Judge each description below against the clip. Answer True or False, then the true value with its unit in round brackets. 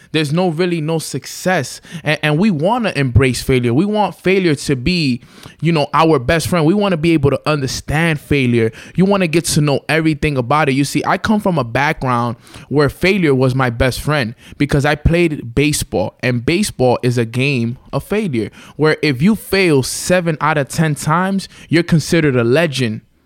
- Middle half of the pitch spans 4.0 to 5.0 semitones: True (4.5 semitones)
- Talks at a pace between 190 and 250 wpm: True (195 wpm)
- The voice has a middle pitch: True (150 Hz)